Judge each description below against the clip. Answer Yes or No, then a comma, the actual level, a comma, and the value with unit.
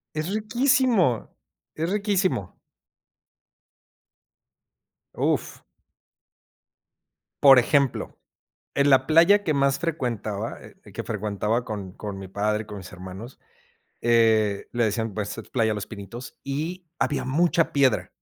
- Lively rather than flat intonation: Yes, wide, 7.3 semitones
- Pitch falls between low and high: No, low, 120 Hz